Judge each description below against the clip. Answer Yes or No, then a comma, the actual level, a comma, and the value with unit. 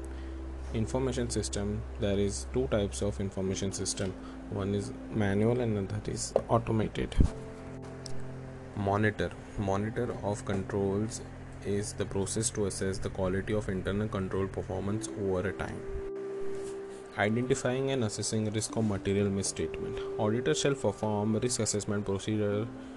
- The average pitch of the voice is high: No, low, 105 Hz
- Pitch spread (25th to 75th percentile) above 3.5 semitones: No, average, 2.7 semitones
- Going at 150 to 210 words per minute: No, average, 125 wpm